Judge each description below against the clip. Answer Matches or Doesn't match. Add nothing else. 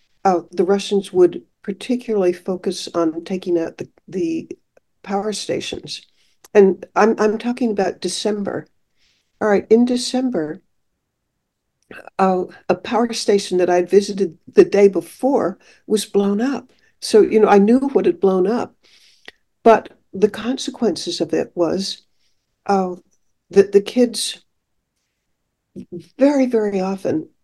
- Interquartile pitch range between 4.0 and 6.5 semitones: Matches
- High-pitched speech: Matches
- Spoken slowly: Matches